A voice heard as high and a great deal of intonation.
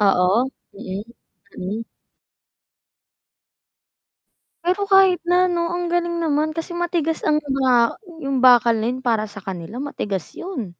Yes: very high, 260 Hz; wide, 8.4 semitones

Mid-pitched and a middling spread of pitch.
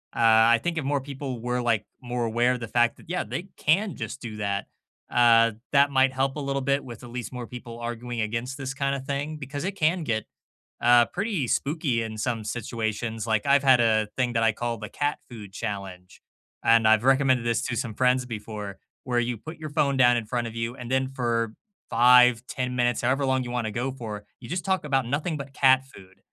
No: low, 125 Hz; average, 3.0 semitones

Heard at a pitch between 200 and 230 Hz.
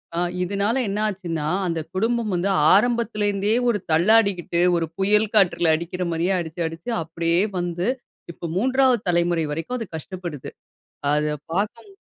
No: medium, 185 Hz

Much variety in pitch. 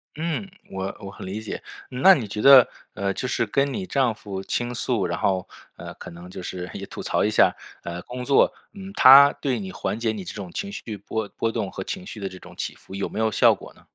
Yes: wide, 5.7 semitones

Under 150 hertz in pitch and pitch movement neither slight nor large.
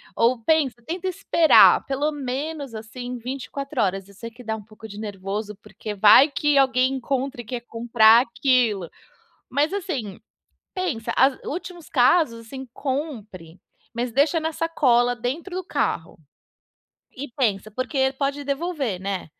No: very high, 255 Hz; average, 4.5 semitones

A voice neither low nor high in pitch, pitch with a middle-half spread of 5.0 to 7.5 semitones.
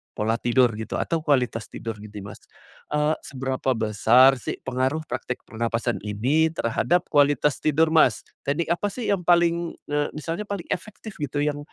Yes: medium, 145 Hz; wide, 5.6 semitones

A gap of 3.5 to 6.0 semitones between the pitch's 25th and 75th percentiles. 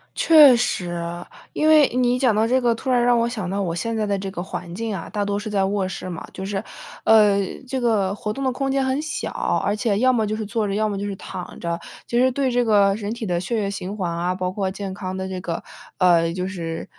Yes: average, 4.1 semitones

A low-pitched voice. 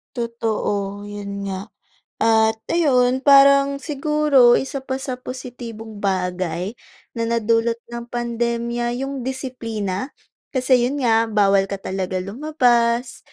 No: high, 235 Hz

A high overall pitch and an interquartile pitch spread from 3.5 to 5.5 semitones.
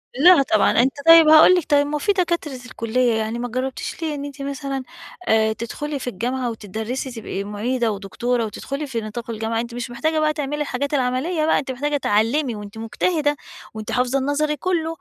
Yes: very high, 260 Hz; average, 4.4 semitones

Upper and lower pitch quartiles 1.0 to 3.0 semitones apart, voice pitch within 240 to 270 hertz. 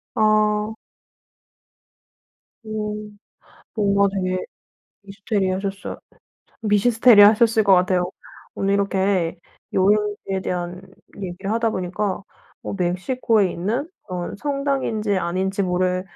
No: narrow, 2.5 semitones; high, 200 Hz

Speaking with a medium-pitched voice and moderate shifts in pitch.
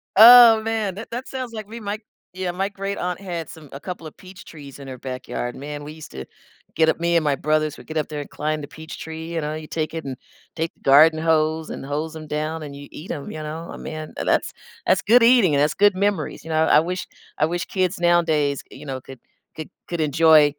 Yes: medium, 160 Hz; average, 3.5 semitones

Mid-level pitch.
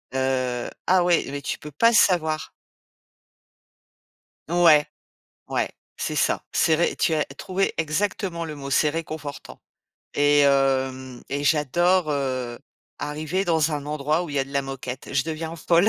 Yes: medium, 150 Hz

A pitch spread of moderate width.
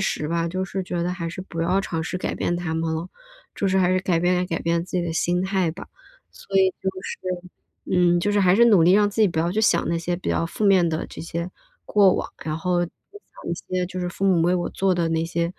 No: narrow, 2.1 semitones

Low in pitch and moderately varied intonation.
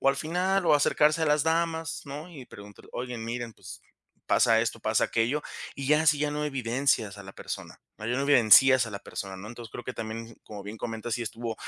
Yes: low, 125 Hz; average, 4.9 semitones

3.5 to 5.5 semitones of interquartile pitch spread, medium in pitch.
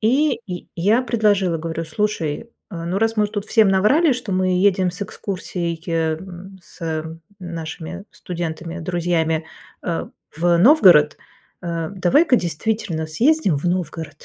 Yes: average, 4.1 semitones; medium, 180 Hz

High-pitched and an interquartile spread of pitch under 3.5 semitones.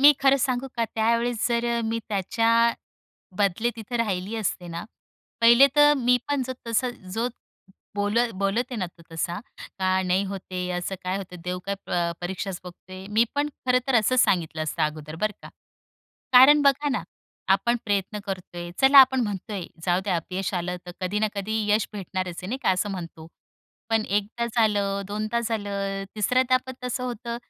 No: high, 210 Hz; average, 4.2 semitones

